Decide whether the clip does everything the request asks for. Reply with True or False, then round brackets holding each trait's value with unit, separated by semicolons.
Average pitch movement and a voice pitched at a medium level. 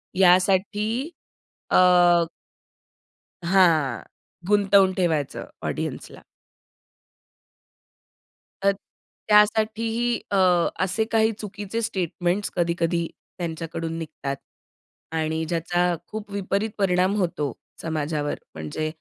True (3.8 semitones; 180 Hz)